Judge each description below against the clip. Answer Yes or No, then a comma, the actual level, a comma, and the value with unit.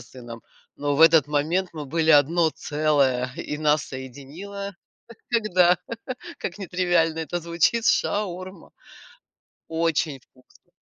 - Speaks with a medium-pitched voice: Yes, medium, 160 Hz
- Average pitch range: Yes, average, 3.6 semitones